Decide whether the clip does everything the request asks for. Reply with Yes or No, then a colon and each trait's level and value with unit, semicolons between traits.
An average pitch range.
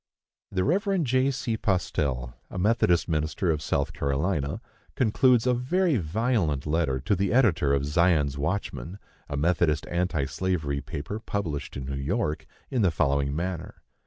No: wide, 7.3 semitones